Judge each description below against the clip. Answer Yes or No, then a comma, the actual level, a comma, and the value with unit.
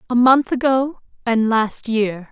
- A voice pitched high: Yes, high, 235 Hz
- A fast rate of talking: No, average, 155 wpm